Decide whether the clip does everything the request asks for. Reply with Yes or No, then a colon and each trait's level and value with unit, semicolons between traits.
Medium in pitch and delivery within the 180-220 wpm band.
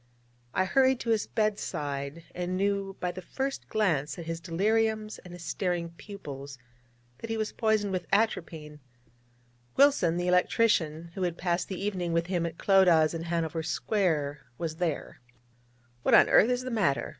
No: medium, 180 Hz; average, 165 wpm